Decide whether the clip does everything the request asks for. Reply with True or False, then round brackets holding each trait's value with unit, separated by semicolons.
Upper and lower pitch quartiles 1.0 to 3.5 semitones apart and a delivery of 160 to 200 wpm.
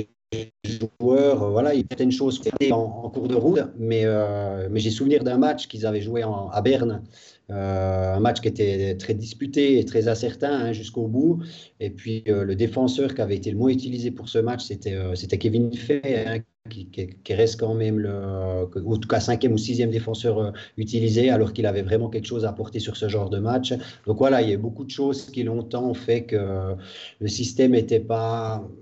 False (2.7 semitones; 210 wpm)